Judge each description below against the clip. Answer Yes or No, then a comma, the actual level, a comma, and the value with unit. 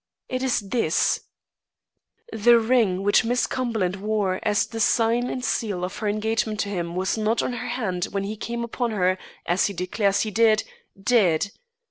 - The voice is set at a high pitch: Yes, high, 215 Hz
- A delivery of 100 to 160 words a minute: No, average, 175 wpm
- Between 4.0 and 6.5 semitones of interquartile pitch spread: No, average, 3.4 semitones